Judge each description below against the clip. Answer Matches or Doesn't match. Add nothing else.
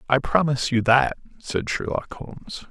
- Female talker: Doesn't match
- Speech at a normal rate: Matches